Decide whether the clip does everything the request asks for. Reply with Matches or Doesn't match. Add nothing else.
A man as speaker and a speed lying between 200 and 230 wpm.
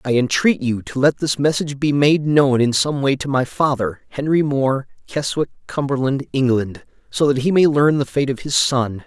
Matches